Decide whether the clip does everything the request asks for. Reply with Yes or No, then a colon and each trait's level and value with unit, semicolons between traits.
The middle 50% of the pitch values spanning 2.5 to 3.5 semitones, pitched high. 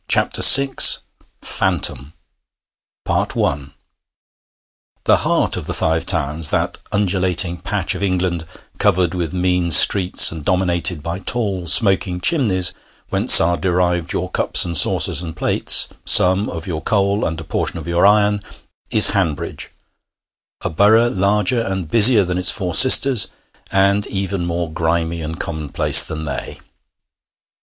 No: average, 3.2 semitones; very low, 90 Hz